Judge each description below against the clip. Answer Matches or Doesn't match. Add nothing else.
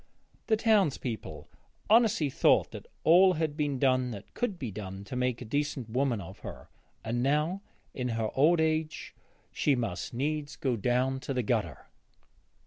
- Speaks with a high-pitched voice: Doesn't match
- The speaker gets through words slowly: Doesn't match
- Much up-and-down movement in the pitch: Doesn't match